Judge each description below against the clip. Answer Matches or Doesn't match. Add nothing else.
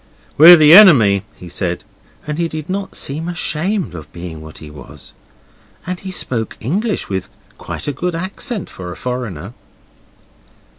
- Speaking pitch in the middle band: Matches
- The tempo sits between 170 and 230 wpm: Doesn't match